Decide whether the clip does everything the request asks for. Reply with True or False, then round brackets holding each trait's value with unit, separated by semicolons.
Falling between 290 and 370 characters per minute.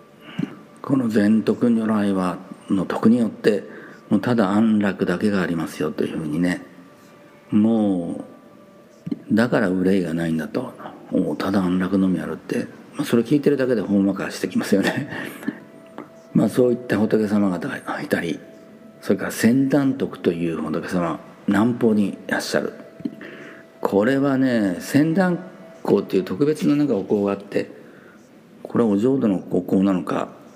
True (295 characters per minute)